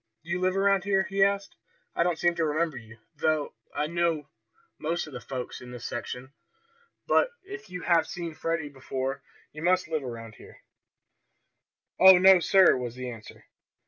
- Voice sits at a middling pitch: Yes, medium, 160 Hz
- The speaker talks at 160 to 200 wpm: Yes, average, 175 wpm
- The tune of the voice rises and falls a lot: Yes, wide, 5.7 semitones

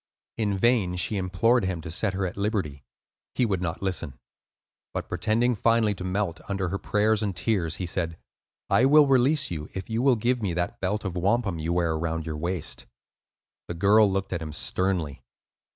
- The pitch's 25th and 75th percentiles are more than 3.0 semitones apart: Yes, average, 4.2 semitones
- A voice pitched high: No, very low, 95 Hz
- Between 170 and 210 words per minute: Yes, average, 190 wpm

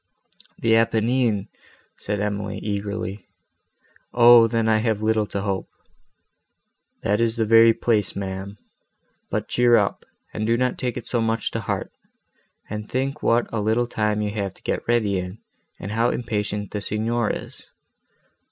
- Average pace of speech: Yes, average, 155 wpm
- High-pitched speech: No, low, 110 Hz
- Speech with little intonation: Yes, narrow, 2.1 semitones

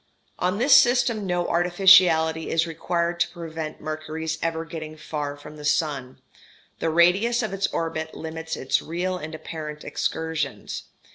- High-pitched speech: No, medium, 165 Hz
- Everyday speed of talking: Yes, average, 150 wpm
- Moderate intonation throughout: No, narrow, 2.2 semitones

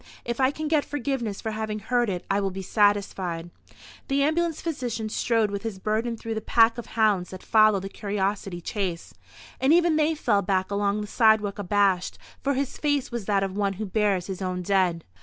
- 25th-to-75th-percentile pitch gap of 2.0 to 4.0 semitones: Yes, average, 3.5 semitones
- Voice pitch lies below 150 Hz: No, high, 210 Hz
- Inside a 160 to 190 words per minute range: No, average, 200 wpm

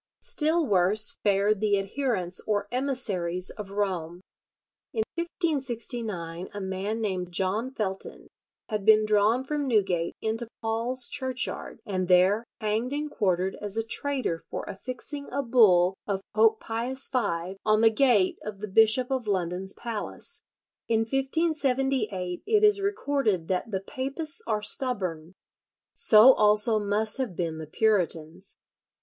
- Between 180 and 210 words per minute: No, slow, 135 wpm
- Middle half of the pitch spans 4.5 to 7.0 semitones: Yes, average, 5.1 semitones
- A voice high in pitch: Yes, high, 215 Hz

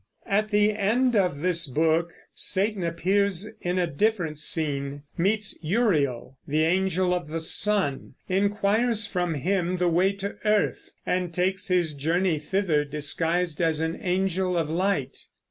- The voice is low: No, medium, 180 Hz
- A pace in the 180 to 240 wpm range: No, average, 145 wpm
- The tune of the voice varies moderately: Yes, average, 3.7 semitones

